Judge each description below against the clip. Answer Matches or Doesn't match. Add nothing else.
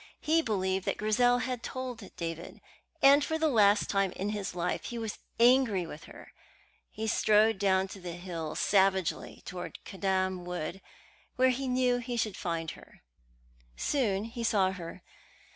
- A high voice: Matches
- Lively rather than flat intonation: Doesn't match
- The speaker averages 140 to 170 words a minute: Matches